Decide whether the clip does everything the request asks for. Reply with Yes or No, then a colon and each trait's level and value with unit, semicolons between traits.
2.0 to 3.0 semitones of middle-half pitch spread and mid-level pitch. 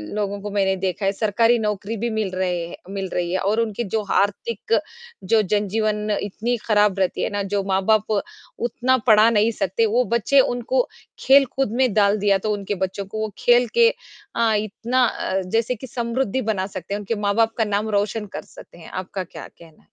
No: average, 2.7 semitones; high, 210 Hz